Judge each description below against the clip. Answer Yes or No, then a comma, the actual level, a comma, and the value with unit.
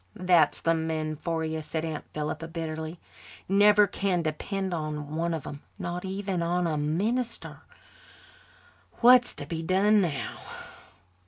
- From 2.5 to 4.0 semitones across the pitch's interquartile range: Yes, average, 3.5 semitones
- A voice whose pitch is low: No, medium, 165 Hz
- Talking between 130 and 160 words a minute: Yes, average, 140 wpm